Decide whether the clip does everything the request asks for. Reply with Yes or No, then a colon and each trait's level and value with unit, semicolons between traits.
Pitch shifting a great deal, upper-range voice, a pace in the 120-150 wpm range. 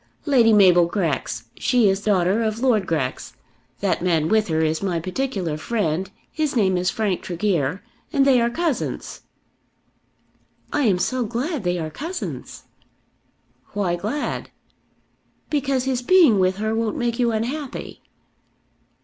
Yes: wide, 5.9 semitones; high, 210 Hz; average, 140 wpm